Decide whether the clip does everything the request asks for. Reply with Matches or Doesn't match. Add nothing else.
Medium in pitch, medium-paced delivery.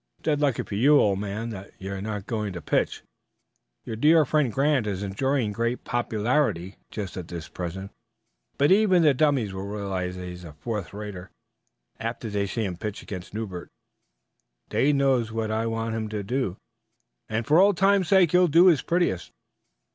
Doesn't match